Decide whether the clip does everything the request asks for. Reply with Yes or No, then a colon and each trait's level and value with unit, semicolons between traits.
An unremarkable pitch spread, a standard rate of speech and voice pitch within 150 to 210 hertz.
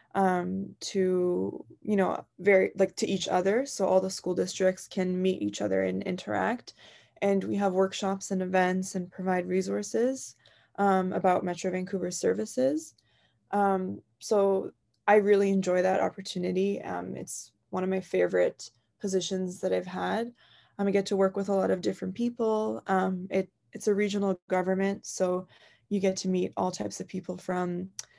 No: narrow, 1.5 semitones; average, 165 wpm; high, 190 Hz